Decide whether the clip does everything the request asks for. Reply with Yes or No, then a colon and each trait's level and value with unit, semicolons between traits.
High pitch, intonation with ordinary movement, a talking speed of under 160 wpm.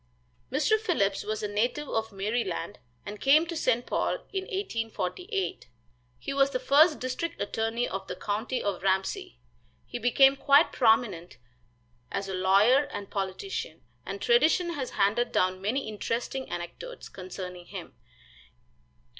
No: high, 230 Hz; wide, 6.2 semitones; average, 140 wpm